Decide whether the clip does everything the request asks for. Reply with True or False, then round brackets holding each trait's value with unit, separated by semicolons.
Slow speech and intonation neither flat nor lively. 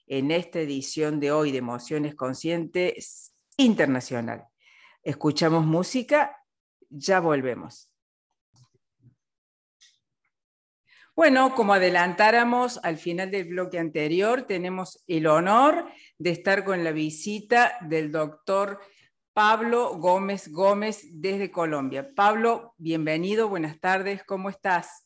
True (100 wpm; 4.7 semitones)